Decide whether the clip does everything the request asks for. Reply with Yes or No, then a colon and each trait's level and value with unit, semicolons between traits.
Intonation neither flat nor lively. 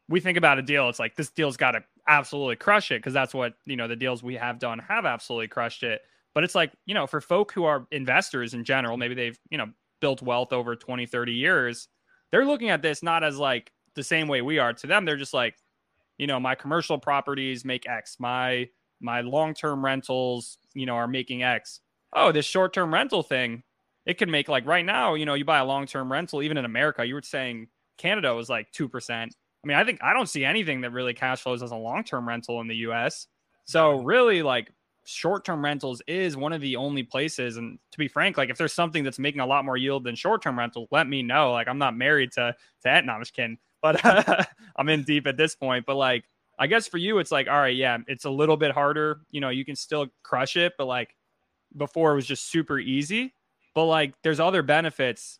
Yes: average, 3.7 semitones